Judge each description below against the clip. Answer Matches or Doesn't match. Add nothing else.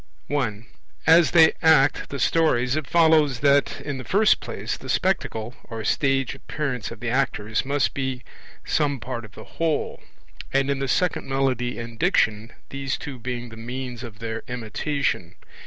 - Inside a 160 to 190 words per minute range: Matches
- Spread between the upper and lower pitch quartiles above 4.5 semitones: Doesn't match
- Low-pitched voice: Matches